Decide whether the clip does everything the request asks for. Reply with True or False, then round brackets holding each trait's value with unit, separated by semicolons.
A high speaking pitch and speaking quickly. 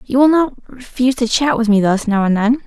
True (240 Hz; 270 wpm)